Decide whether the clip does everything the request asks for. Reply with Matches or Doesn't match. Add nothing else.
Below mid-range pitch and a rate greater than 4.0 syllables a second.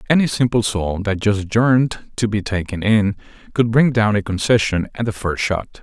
Matches